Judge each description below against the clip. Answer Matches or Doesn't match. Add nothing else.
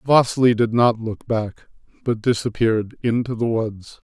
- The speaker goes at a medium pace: Matches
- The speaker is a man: Matches